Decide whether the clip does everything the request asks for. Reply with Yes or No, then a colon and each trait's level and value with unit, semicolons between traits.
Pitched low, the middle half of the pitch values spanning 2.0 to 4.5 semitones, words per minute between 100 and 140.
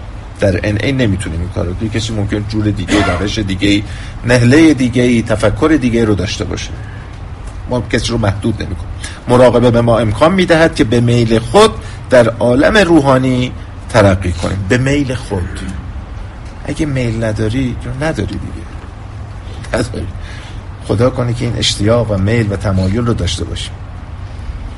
No: low, 105 Hz; average, 3.7 semitones; average, 150 wpm